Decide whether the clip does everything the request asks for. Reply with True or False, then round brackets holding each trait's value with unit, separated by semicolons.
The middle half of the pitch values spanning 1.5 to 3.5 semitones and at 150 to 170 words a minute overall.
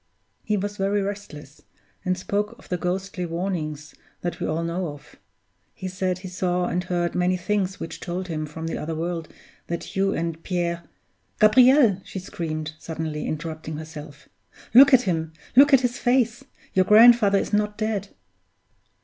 False (3.9 semitones; 165 wpm)